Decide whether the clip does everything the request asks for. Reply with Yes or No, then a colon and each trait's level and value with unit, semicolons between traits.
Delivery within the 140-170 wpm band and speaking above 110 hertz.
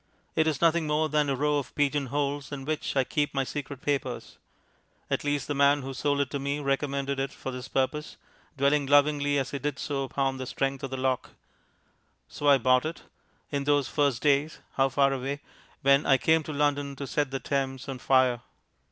No: fast, 205 wpm; medium, 140 Hz